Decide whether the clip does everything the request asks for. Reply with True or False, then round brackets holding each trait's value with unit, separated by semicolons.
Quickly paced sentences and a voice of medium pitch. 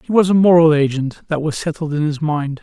True (230 wpm; 155 Hz)